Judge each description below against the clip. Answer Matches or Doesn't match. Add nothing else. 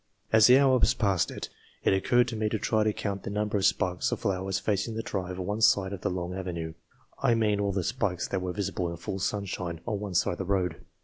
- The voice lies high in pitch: Doesn't match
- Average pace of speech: Doesn't match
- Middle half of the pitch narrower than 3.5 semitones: Matches